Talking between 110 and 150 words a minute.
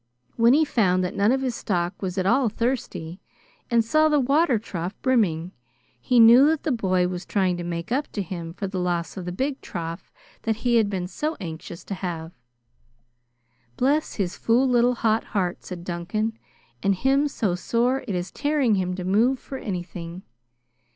No: average, 185 wpm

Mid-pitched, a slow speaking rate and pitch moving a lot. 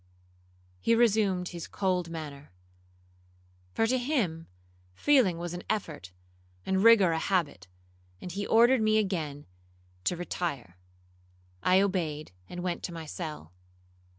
No: medium, 180 Hz; slow, 125 wpm; average, 4.3 semitones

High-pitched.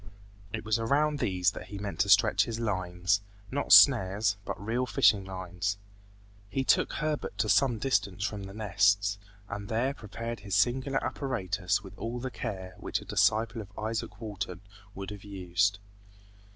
No: low, 105 Hz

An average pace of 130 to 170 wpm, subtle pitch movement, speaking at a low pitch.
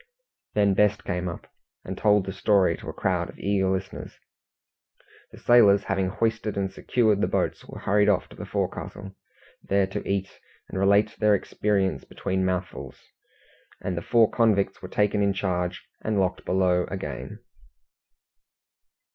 Yes: average, 155 wpm; narrow, 1.8 semitones; low, 100 Hz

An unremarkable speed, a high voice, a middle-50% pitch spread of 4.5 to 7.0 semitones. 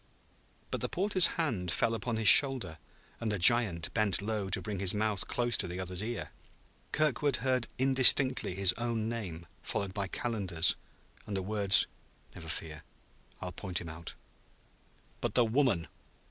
No: average, 160 wpm; low, 105 Hz; average, 4.8 semitones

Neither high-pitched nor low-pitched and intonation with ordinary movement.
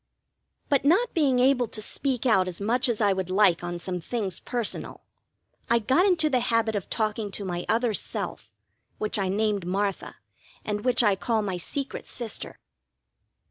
No: high, 220 Hz; average, 4.2 semitones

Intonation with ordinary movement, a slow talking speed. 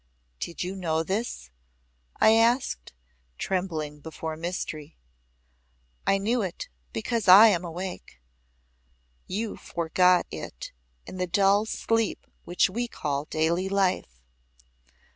Yes: average, 4.0 semitones; slow, 110 wpm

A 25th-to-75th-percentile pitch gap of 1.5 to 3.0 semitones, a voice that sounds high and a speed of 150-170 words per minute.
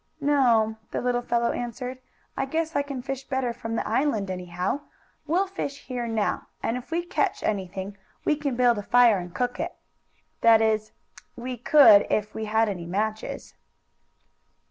No: average, 3.9 semitones; high, 235 Hz; average, 165 wpm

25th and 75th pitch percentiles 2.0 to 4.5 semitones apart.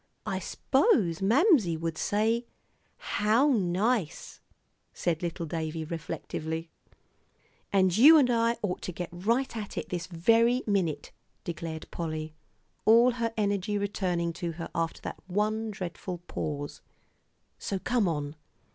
No: average, 5.1 semitones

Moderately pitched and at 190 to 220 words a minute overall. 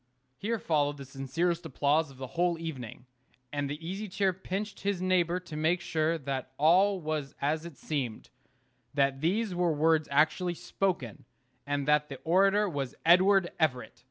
No: medium, 160 Hz; average, 160 wpm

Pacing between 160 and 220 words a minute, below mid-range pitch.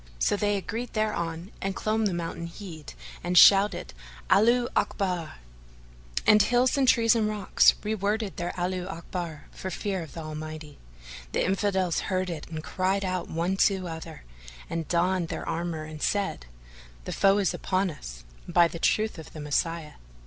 No: average, 165 wpm; medium, 185 Hz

